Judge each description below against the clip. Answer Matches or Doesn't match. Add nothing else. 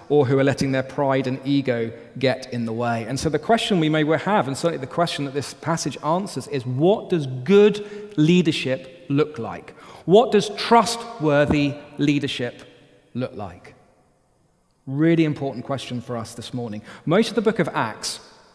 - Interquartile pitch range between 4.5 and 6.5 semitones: Matches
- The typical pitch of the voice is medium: Matches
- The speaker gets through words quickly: Doesn't match